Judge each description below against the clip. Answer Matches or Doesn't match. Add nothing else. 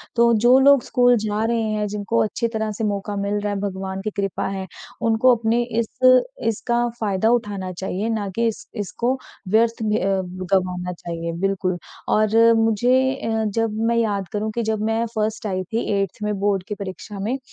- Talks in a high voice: Matches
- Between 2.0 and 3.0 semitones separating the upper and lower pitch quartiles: Matches